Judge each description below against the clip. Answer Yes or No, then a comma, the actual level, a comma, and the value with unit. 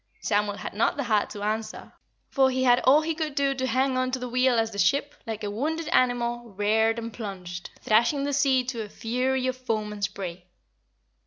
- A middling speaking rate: No, fast, 215 wpm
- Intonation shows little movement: No, average, 3.7 semitones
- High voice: Yes, high, 240 Hz